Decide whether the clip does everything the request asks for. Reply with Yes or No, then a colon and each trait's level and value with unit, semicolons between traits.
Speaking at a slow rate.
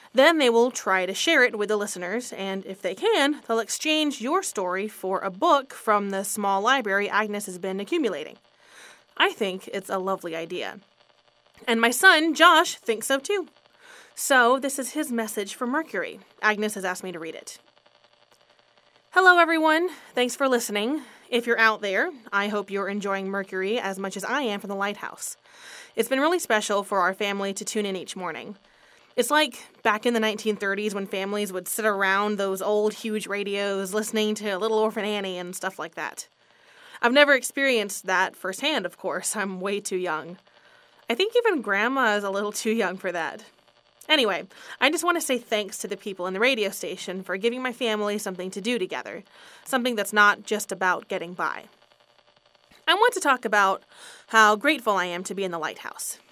No: average, 190 wpm